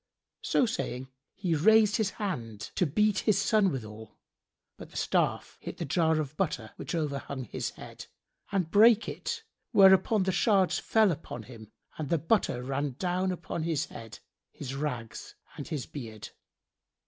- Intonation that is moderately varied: No, wide, 6.7 semitones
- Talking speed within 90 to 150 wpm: No, average, 160 wpm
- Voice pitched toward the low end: No, medium, 160 Hz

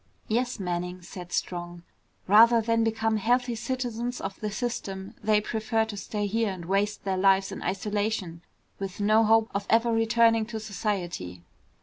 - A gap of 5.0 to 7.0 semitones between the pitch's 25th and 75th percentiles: No, average, 2.8 semitones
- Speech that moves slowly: No, average, 155 wpm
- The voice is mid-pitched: No, high, 210 Hz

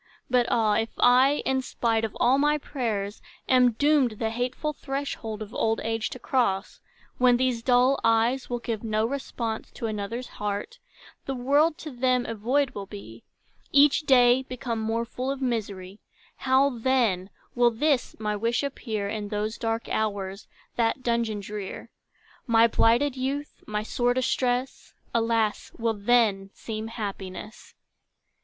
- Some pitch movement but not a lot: Yes, average, 3.0 semitones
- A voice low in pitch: No, high, 235 Hz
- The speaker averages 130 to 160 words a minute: Yes, average, 150 wpm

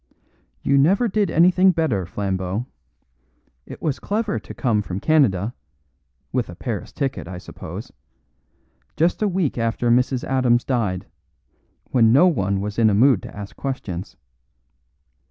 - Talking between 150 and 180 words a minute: No, average, 140 wpm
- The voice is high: No, low, 120 Hz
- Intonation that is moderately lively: No, wide, 7.6 semitones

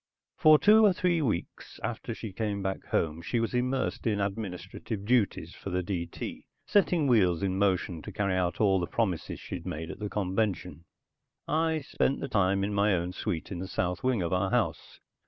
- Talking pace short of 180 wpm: No, average, 190 wpm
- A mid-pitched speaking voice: No, low, 100 Hz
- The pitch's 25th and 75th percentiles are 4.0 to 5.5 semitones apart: Yes, average, 4.6 semitones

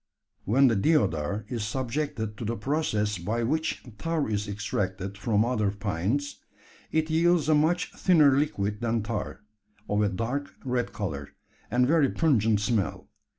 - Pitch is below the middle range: Yes, low, 115 Hz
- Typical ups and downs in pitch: No, wide, 5.8 semitones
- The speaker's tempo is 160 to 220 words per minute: No, average, 150 wpm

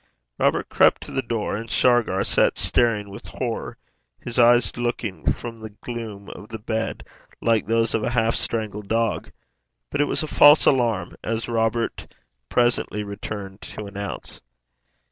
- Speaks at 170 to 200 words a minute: No, average, 155 wpm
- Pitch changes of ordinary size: No, narrow, 2.3 semitones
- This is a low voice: Yes, low, 115 Hz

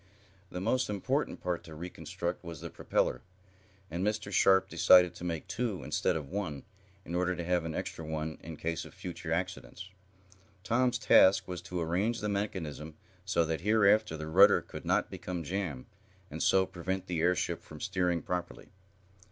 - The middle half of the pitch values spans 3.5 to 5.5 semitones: No, average, 3.0 semitones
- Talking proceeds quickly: No, average, 170 wpm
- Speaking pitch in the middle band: No, very low, 90 Hz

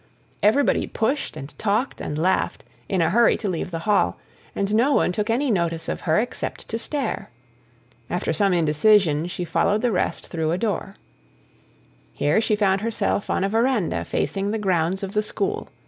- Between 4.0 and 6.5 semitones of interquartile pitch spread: Yes, average, 4.6 semitones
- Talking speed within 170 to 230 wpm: Yes, average, 180 wpm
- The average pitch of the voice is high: Yes, high, 200 Hz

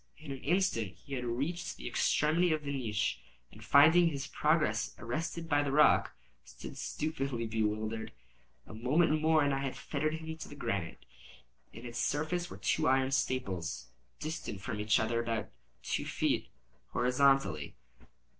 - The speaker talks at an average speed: Yes, average, 155 wpm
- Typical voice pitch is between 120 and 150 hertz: Yes, low, 135 Hz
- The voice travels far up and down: Yes, wide, 5.7 semitones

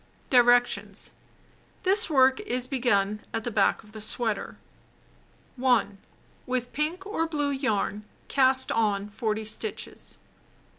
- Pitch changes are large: No, average, 4.4 semitones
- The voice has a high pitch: Yes, high, 245 Hz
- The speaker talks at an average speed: No, slow, 115 wpm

